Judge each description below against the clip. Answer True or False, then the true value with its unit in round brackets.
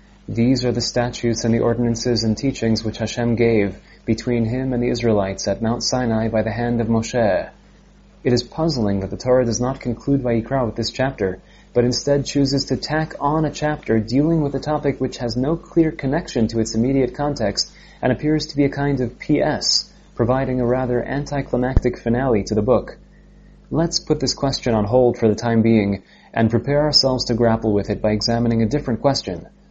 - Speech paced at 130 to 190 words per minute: False (200 wpm)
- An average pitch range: True (3.2 semitones)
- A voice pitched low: True (120 Hz)